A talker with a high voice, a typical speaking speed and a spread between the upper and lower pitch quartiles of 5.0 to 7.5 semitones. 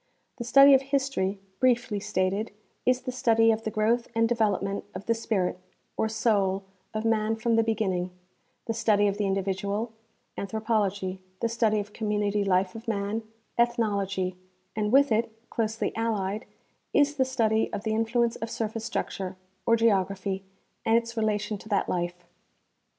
No: high, 220 Hz; average, 160 wpm; narrow, 2.5 semitones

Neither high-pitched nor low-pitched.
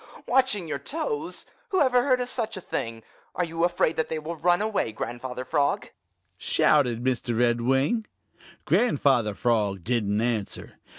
Yes: medium, 145 Hz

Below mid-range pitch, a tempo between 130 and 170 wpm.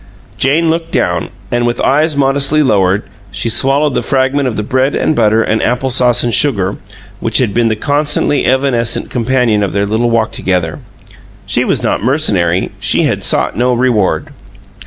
No: low, 120 Hz; average, 180 wpm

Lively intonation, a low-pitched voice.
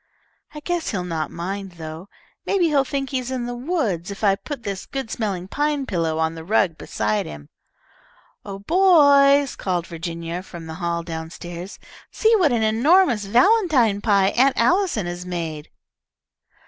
No: wide, 8.4 semitones; high, 200 Hz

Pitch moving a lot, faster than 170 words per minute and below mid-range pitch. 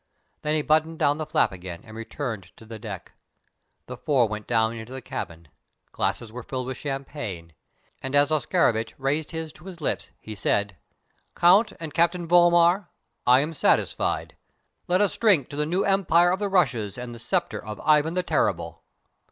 No: wide, 6.9 semitones; average, 180 wpm; medium, 145 Hz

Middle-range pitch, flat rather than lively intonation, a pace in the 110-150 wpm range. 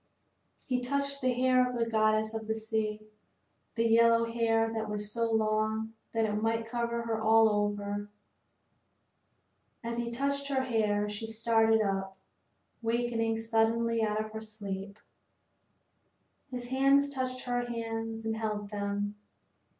No: high, 225 Hz; narrow, 1.5 semitones; average, 140 wpm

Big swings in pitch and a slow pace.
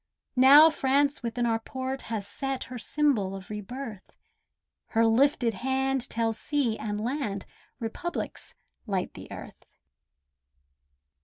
No: average, 3.7 semitones; slow, 125 wpm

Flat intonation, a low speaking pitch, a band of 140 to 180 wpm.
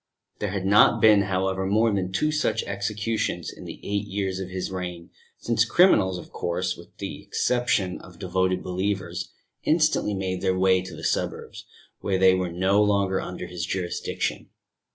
Yes: narrow, 1.9 semitones; very low, 95 Hz; average, 170 wpm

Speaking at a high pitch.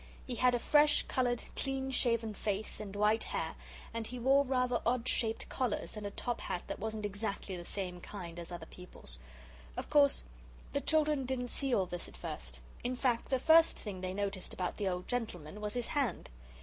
Yes: high, 225 Hz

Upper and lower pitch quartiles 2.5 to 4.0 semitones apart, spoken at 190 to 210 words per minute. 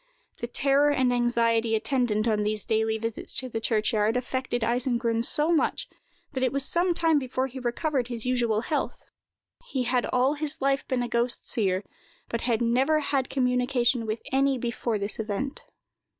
No: average, 2.8 semitones; average, 170 wpm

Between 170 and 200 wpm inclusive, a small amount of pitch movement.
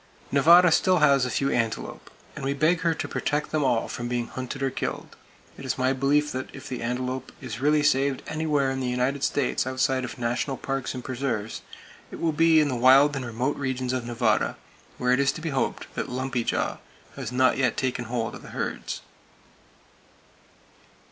Yes: average, 195 wpm; narrow, 2.3 semitones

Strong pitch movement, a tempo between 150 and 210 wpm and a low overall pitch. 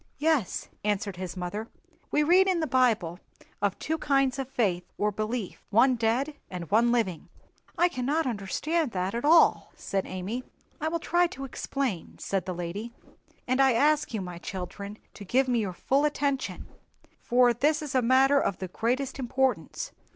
No: wide, 5.8 semitones; average, 170 wpm; high, 245 Hz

